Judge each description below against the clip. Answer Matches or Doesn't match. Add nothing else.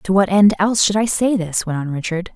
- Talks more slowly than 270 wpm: Doesn't match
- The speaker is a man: Doesn't match